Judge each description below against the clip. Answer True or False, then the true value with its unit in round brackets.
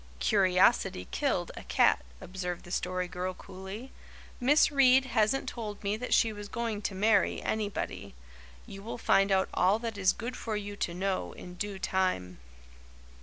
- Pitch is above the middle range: True (200 Hz)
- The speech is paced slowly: False (165 wpm)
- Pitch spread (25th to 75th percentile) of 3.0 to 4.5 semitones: True (3.4 semitones)